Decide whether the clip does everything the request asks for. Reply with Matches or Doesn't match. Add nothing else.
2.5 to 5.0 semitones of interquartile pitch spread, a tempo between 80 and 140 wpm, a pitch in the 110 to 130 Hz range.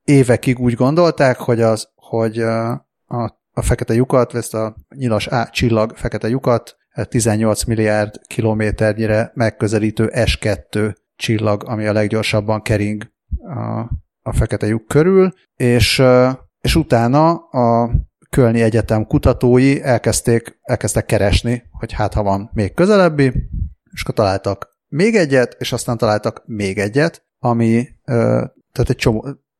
Matches